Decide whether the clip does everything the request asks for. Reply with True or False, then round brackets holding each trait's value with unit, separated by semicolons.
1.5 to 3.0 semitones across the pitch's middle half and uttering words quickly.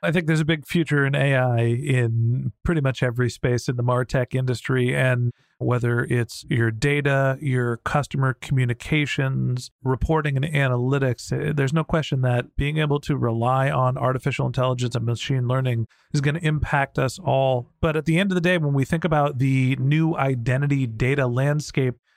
False (2.6 semitones; 175 wpm)